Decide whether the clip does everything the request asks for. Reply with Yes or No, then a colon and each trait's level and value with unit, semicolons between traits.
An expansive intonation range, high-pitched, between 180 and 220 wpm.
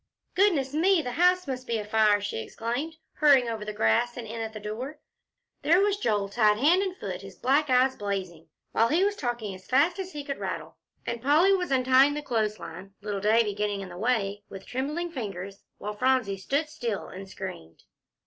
Yes: wide, 6.2 semitones; high, 235 Hz; average, 200 wpm